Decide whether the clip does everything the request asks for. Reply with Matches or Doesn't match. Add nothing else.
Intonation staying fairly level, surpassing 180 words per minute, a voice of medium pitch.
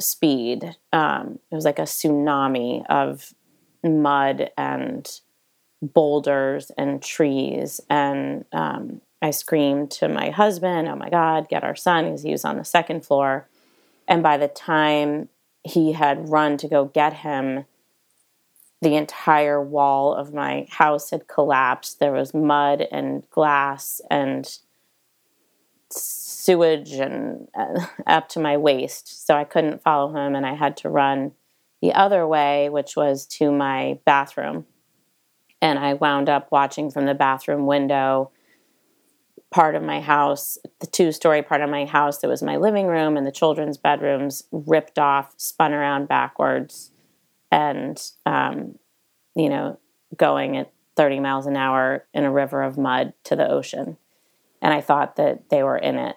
Doesn't match